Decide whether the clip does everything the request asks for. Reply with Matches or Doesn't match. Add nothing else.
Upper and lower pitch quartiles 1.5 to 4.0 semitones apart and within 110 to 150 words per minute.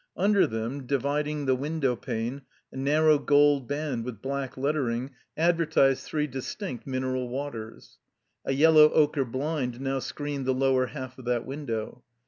Matches